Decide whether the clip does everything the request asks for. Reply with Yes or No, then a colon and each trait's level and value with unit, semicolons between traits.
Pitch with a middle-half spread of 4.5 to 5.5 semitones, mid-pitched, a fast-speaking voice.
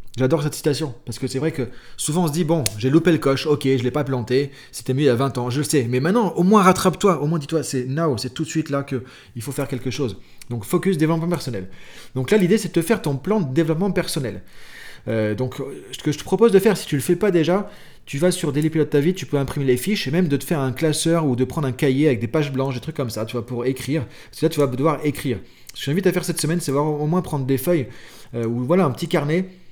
Yes: average, 4.8 semitones; medium, 150 Hz; fast, 300 wpm